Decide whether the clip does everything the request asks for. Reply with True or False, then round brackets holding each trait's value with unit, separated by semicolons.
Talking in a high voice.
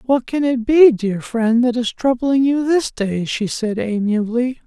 True (240 Hz)